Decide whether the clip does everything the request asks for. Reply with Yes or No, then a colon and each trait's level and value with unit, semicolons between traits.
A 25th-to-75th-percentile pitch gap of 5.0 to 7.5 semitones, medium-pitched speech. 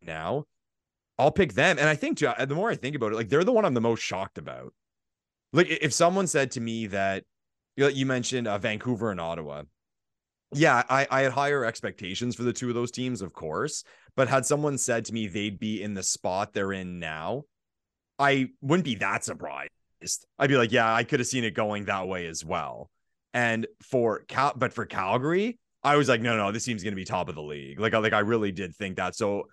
No: wide, 5.4 semitones; low, 115 Hz